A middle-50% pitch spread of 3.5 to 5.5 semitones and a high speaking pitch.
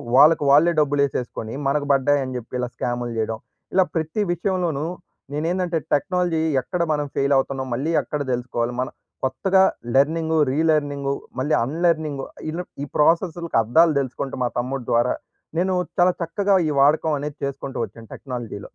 No: average, 4.1 semitones; medium, 145 Hz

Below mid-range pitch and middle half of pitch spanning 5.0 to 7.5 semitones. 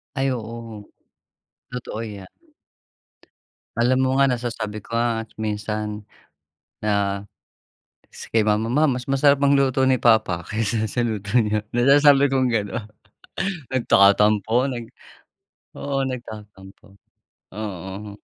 No: low, 115 Hz; average, 3.4 semitones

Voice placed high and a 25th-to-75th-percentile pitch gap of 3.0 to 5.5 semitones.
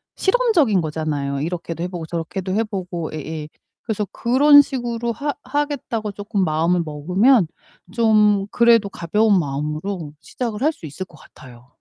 No: high, 195 Hz; wide, 6.6 semitones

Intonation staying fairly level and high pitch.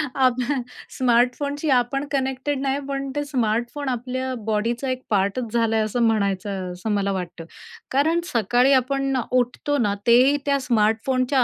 No: average, 3.7 semitones; very high, 250 Hz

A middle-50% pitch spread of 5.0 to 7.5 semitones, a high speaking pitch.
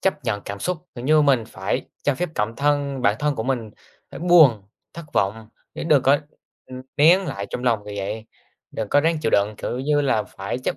No: wide, 5.5 semitones; low, 130 Hz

